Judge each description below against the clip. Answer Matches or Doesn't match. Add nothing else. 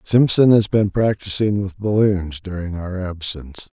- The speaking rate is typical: Matches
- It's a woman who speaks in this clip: Doesn't match